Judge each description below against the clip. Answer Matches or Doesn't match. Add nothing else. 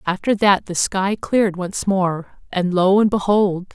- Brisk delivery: Doesn't match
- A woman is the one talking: Matches